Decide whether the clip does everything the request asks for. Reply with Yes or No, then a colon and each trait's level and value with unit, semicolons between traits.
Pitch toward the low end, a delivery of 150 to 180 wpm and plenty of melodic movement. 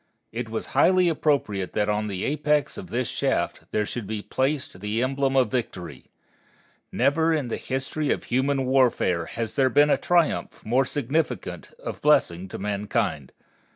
Yes: low, 130 Hz; average, 160 wpm; wide, 5.7 semitones